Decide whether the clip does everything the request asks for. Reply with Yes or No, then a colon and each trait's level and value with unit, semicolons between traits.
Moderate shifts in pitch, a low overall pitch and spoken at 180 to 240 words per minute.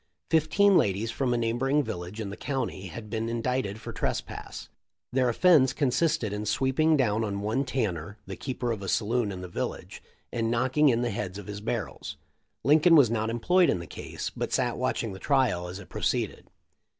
Yes: average, 4.5 semitones; low, 115 Hz; average, 200 wpm